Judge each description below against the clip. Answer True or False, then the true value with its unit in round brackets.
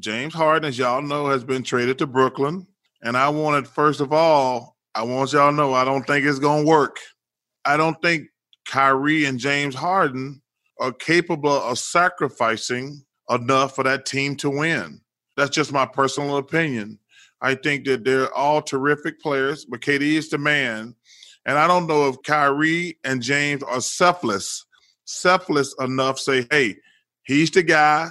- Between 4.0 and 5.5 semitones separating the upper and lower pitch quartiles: False (2.6 semitones)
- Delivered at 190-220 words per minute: False (165 wpm)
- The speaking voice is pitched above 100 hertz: True (140 Hz)